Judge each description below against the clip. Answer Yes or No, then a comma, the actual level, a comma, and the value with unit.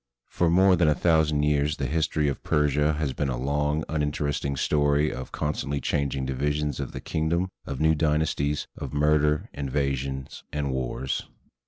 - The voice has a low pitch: Yes, very low, 75 Hz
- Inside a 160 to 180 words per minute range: Yes, average, 170 wpm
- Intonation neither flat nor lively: No, narrow, 1.6 semitones